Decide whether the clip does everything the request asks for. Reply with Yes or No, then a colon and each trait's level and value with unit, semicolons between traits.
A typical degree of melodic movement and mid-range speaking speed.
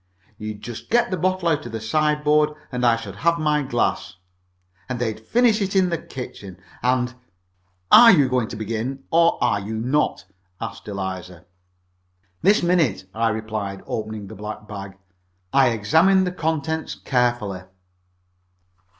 No: wide, 7.0 semitones; average, 150 wpm